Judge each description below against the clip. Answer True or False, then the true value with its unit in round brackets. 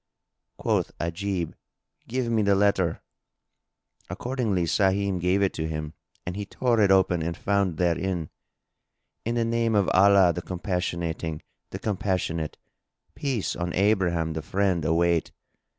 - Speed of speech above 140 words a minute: False (135 wpm)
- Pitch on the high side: False (95 Hz)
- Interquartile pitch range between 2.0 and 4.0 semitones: True (3.1 semitones)